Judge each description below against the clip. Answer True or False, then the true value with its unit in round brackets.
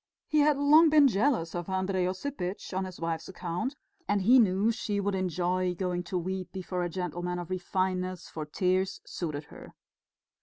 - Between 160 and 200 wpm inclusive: True (175 wpm)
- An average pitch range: False (2.2 semitones)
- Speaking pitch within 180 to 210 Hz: True (185 Hz)